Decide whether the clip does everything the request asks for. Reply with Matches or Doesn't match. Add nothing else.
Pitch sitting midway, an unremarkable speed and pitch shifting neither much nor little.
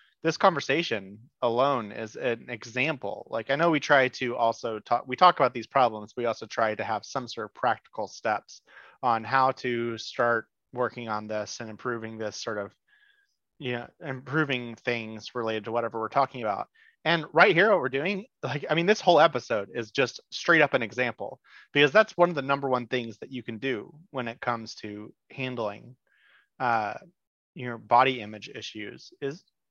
Doesn't match